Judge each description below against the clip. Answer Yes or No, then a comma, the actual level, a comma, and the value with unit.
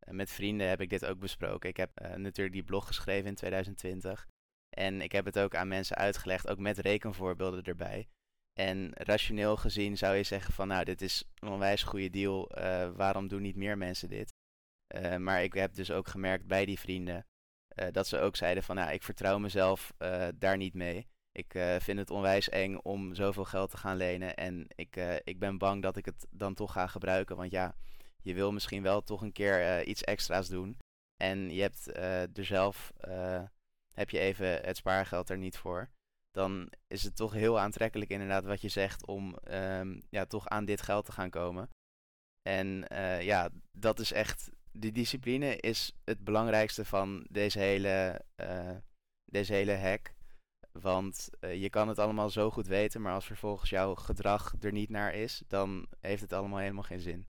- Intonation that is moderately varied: No, narrow, 1.6 semitones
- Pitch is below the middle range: Yes, very low, 95 Hz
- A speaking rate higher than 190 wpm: Yes, fast, 200 wpm